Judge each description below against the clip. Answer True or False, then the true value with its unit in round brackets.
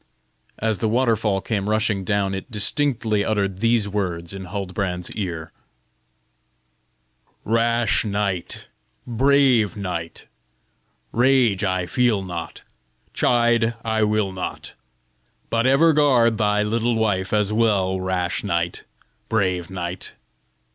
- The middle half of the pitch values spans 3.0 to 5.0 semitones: True (3.5 semitones)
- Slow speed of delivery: True (110 wpm)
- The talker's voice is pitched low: True (105 Hz)